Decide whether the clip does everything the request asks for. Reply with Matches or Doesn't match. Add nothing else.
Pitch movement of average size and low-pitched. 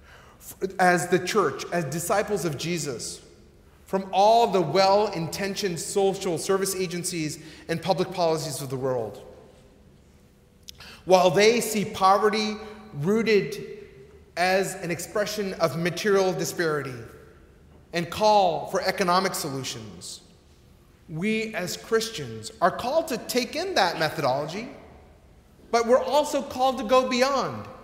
Doesn't match